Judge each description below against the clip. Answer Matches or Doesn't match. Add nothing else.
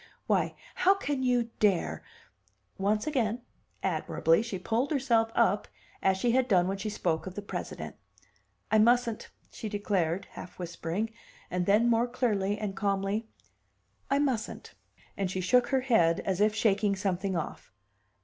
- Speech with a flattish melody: Doesn't match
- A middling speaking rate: Matches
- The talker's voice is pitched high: Matches